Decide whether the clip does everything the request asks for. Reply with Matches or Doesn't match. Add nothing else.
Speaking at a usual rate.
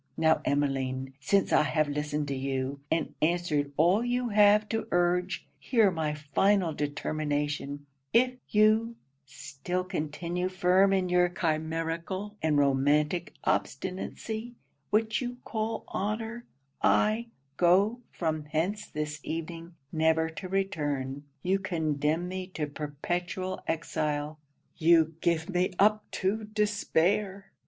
Doesn't match